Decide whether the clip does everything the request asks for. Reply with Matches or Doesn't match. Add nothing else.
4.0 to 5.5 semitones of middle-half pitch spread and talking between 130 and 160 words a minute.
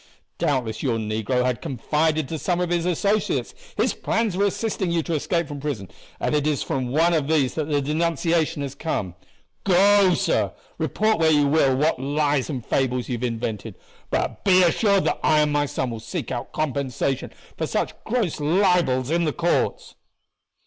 Doesn't match